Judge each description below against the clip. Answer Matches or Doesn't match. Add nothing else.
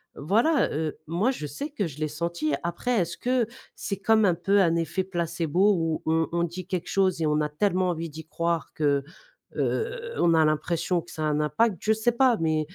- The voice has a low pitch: Doesn't match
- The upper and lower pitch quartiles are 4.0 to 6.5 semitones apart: Matches